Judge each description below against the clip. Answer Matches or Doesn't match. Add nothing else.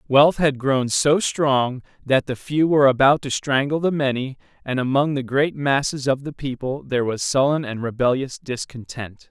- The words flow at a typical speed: Matches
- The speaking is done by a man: Matches